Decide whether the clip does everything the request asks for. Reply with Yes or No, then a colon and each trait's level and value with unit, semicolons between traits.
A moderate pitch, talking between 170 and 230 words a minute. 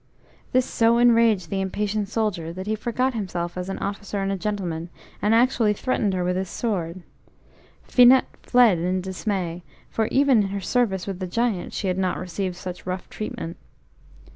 No: high, 195 Hz; average, 175 wpm